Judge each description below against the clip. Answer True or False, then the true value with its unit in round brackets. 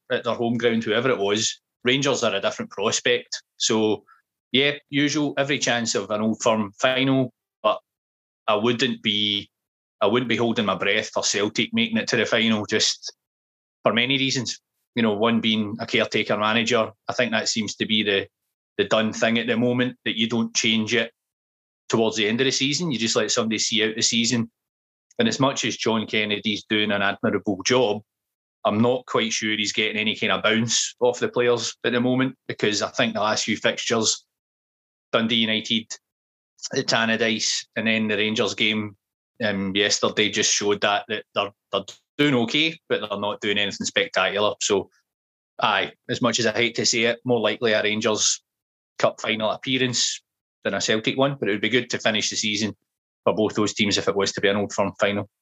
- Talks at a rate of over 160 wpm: True (200 wpm)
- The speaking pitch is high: False (115 Hz)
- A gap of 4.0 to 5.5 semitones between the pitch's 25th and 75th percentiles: False (2.7 semitones)